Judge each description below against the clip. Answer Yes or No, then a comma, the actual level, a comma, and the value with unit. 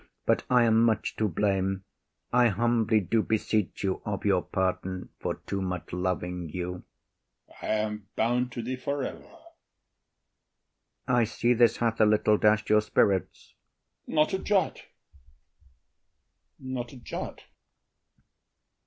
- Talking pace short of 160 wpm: Yes, average, 140 wpm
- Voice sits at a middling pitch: No, low, 110 Hz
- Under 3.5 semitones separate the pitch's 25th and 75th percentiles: No, average, 3.9 semitones